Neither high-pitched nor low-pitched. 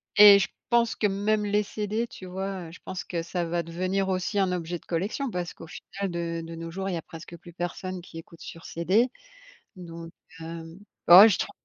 Yes: medium, 180 Hz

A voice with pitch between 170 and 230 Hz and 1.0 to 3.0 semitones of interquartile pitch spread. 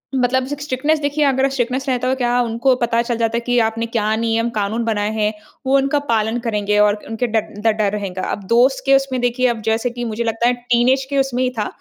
No: high, 240 Hz; average, 2.7 semitones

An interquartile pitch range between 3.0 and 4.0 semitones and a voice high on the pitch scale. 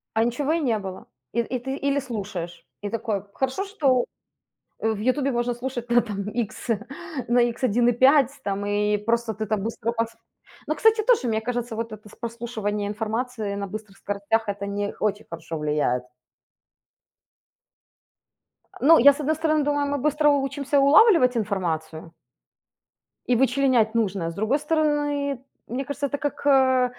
No: average, 4.9 semitones; high, 235 Hz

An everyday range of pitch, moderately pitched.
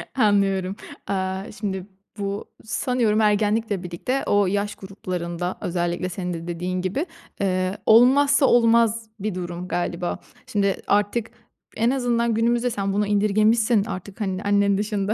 No: average, 3.2 semitones; high, 205 Hz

